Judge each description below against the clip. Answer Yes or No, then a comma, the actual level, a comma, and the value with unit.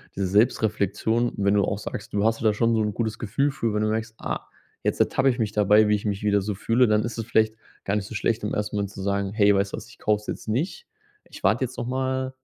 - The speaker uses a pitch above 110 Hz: No, low, 105 Hz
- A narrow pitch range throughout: Yes, narrow, 2.2 semitones